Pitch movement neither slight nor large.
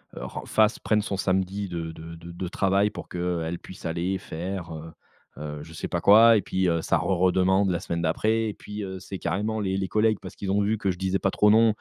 Yes: average, 3.1 semitones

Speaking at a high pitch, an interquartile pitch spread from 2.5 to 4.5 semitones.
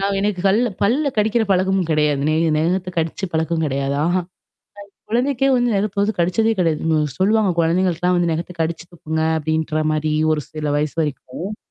No: medium, 175 Hz; average, 4.1 semitones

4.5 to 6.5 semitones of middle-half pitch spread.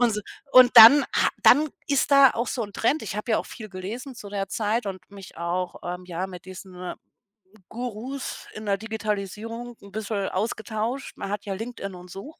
No: average, 3.8 semitones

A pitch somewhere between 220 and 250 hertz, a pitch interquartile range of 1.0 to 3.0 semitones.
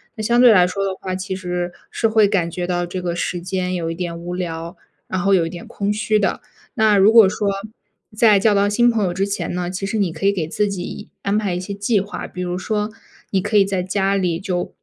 No: high, 190 Hz; narrow, 2.5 semitones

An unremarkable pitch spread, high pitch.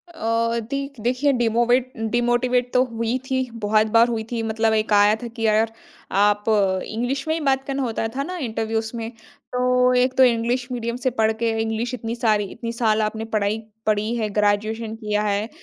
No: narrow, 2.2 semitones; high, 230 Hz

